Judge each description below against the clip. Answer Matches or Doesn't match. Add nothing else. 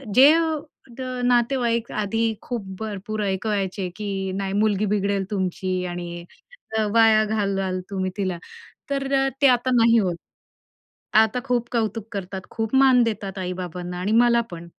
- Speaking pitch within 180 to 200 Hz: Doesn't match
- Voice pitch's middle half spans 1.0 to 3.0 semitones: Doesn't match